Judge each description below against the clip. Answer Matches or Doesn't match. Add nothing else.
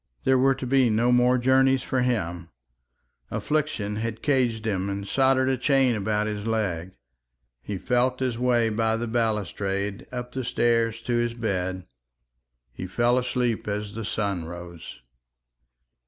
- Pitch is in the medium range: Doesn't match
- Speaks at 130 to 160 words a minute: Matches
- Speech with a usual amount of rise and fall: Matches